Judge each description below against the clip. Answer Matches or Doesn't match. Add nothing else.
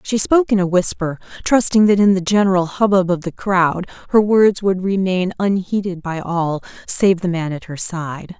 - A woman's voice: Matches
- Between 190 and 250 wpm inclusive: Matches